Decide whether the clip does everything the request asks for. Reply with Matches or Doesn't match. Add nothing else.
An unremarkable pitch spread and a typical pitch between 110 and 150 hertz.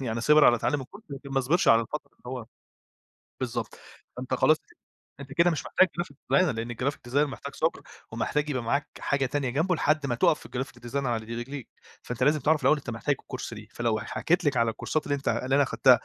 Matches